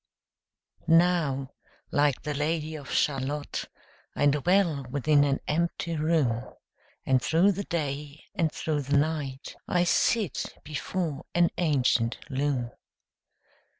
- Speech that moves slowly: Yes, slow, 115 wpm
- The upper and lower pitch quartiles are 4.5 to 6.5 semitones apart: No, average, 3.1 semitones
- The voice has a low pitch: No, medium, 150 Hz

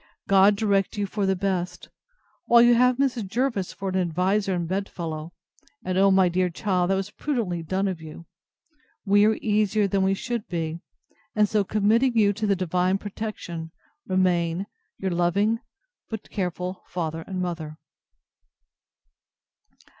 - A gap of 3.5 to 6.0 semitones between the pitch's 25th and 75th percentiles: No, average, 2.9 semitones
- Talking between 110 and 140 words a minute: No, average, 155 wpm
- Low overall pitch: No, high, 195 Hz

